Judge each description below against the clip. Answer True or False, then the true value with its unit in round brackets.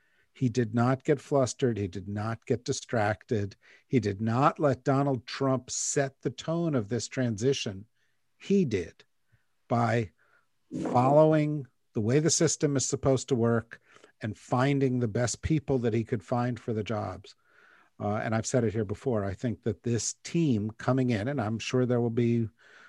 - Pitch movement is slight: False (3.4 semitones)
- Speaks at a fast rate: False (175 wpm)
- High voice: False (125 Hz)